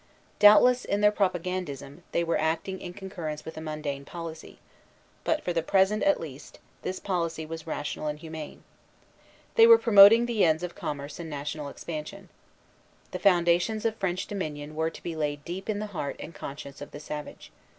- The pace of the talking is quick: No, average, 180 wpm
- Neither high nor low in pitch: Yes, medium, 170 Hz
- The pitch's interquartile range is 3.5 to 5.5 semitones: Yes, average, 4.5 semitones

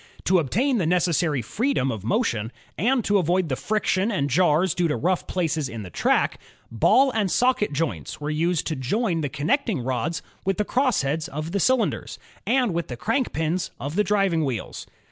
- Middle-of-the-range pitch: Yes, medium, 170 Hz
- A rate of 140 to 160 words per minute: No, average, 190 wpm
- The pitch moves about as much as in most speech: No, wide, 6.1 semitones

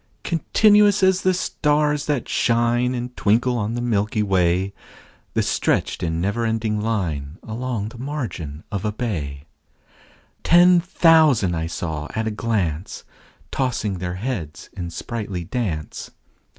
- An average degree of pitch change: No, wide, 6.1 semitones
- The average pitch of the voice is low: Yes, low, 110 Hz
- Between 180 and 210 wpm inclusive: No, slow, 135 wpm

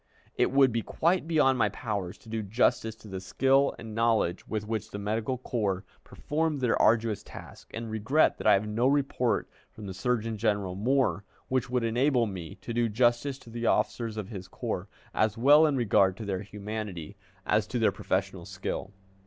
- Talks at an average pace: Yes, average, 190 wpm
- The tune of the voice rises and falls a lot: No, average, 3.6 semitones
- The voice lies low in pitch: Yes, low, 110 Hz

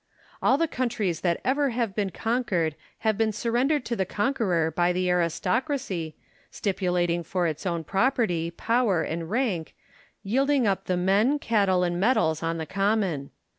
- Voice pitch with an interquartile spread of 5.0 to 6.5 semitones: Yes, wide, 5.4 semitones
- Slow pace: No, average, 155 wpm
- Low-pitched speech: No, high, 195 Hz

